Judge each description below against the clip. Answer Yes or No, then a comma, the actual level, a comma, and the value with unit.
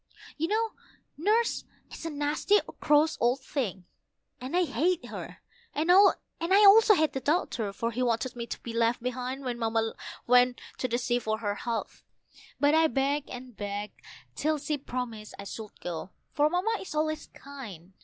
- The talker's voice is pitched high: Yes, very high, 260 Hz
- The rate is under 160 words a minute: No, average, 165 wpm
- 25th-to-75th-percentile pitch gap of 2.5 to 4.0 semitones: No, average, 5.2 semitones